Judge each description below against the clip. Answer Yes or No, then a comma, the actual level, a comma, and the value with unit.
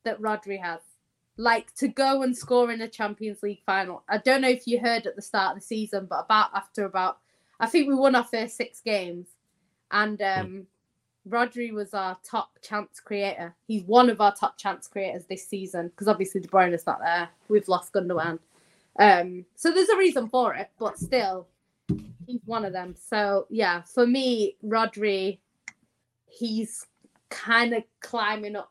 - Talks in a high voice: Yes, high, 210 Hz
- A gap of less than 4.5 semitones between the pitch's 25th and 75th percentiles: Yes, average, 3.4 semitones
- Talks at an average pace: Yes, average, 180 wpm